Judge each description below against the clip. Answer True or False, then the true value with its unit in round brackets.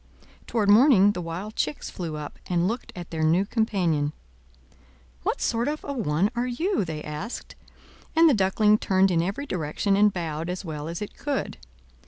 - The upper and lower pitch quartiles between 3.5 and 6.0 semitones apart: True (5.2 semitones)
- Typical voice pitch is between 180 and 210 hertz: True (190 Hz)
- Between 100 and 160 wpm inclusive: False (180 wpm)